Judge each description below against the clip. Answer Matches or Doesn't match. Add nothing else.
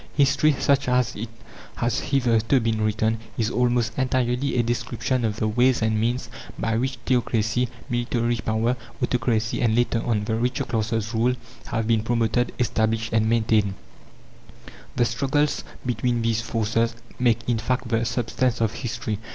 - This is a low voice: Matches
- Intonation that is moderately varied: Doesn't match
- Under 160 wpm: Matches